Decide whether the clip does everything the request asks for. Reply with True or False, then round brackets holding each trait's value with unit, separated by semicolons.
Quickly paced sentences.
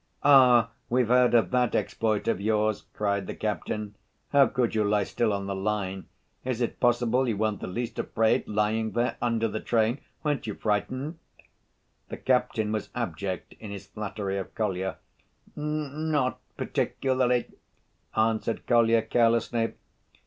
False (150 wpm)